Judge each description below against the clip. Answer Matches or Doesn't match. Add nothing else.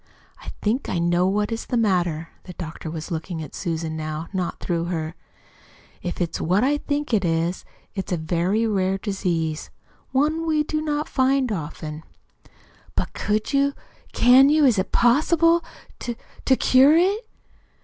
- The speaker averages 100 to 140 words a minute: Doesn't match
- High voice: Matches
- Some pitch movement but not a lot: Doesn't match